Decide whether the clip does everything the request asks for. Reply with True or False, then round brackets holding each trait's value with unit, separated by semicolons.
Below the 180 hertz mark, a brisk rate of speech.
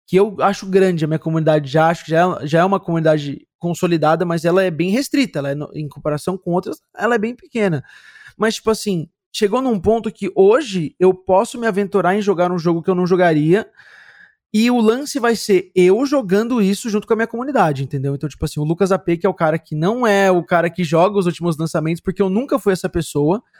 False (185 Hz; 230 wpm)